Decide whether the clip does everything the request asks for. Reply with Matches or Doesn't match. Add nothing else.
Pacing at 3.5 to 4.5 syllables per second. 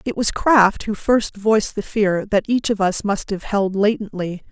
Matches